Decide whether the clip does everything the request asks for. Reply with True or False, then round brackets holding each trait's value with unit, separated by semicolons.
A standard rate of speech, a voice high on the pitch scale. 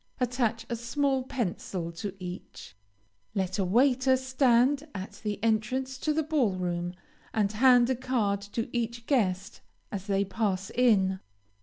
True (145 wpm; 230 Hz)